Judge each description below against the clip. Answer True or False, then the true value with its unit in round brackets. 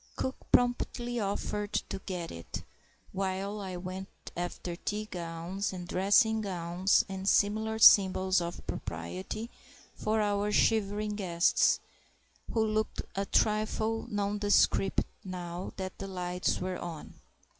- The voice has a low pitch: False (195 Hz)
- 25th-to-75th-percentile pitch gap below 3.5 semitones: True (2.8 semitones)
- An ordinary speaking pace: False (120 wpm)